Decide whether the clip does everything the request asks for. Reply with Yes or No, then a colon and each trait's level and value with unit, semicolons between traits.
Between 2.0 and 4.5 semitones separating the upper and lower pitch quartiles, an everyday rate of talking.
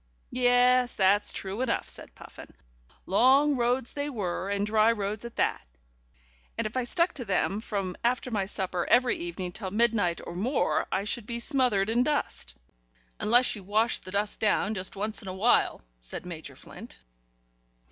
Yes: average, 4.1 semitones; average, 170 wpm